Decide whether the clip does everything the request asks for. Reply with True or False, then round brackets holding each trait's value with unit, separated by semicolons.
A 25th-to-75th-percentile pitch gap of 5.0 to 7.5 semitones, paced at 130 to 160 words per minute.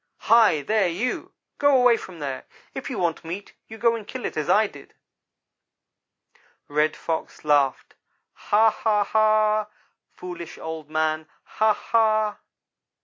True (5.6 semitones; 140 wpm)